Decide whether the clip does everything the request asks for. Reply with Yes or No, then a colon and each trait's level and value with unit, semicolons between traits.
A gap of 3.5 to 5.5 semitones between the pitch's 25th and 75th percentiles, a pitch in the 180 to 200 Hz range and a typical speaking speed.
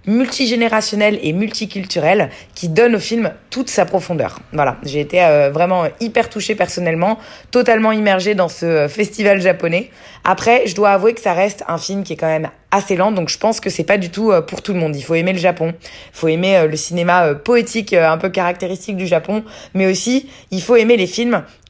Yes: average, 4.4 semitones; high, 190 Hz; average, 200 wpm